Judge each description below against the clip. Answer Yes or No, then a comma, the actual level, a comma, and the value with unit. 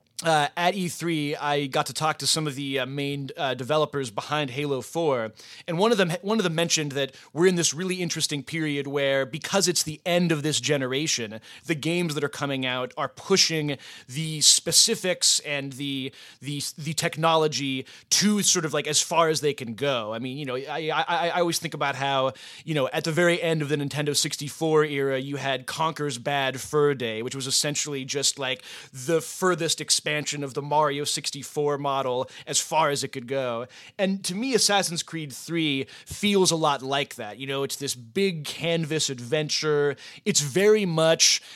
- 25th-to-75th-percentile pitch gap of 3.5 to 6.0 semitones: No, average, 3.1 semitones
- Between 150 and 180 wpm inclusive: No, average, 195 wpm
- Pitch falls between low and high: Yes, medium, 150 Hz